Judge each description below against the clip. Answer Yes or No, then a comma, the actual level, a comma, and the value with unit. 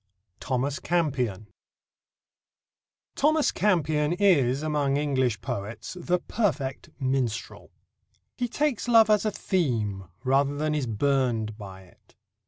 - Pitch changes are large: Yes, wide, 6.6 semitones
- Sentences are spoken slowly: Yes, slow, 110 wpm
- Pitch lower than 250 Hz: Yes, medium, 140 Hz